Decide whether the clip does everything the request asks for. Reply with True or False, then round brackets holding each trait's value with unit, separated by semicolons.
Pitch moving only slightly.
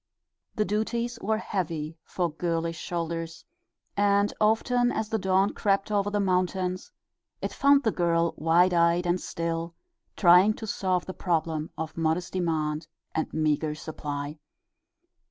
False (3.6 semitones)